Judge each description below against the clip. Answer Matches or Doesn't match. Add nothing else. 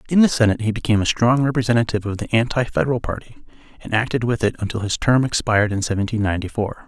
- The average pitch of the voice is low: Matches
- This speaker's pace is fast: Matches